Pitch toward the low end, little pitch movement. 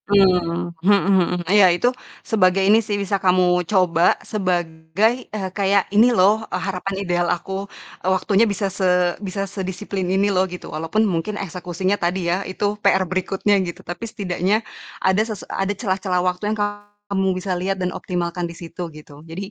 No: high, 190 Hz; narrow, 2.2 semitones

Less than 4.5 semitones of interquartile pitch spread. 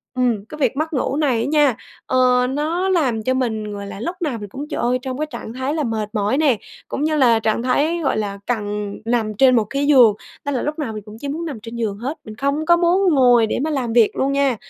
No: average, 4.8 semitones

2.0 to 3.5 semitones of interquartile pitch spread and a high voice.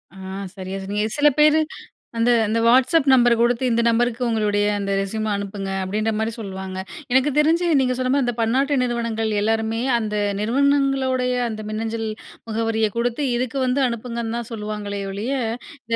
Yes: average, 2.9 semitones; high, 230 Hz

